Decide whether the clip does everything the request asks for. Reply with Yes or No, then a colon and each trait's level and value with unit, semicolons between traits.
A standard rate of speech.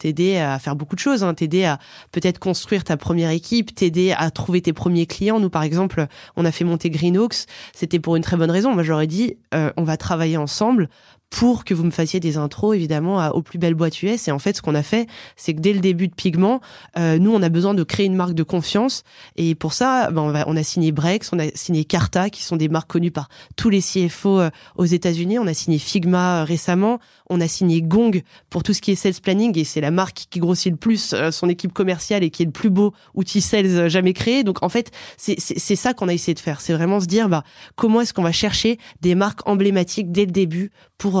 No: fast, 260 wpm